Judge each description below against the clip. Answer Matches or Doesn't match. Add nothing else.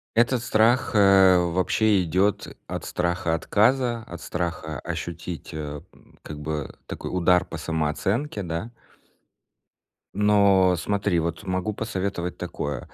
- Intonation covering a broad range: Doesn't match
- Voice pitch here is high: Doesn't match